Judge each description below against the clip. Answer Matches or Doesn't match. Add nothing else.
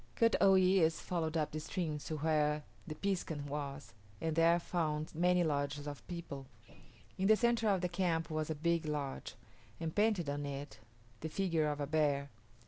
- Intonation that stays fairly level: Doesn't match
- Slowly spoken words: Doesn't match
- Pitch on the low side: Doesn't match